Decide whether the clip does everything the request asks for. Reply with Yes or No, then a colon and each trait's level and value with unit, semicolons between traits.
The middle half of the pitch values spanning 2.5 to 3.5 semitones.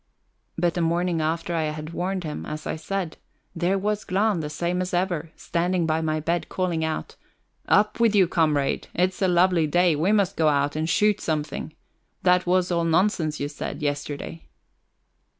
Yes: average, 2.8 semitones